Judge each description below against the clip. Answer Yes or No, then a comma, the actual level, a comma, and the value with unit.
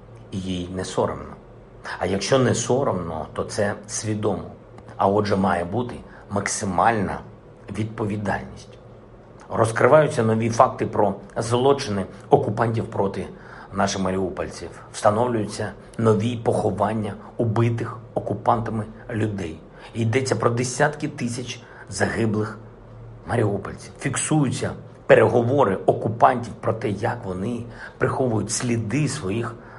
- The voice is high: No, low, 110 Hz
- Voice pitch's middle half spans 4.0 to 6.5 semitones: No, average, 3.1 semitones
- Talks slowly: Yes, slow, 95 wpm